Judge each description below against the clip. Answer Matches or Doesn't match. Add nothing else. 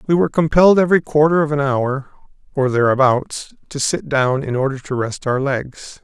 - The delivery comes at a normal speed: Matches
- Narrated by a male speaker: Matches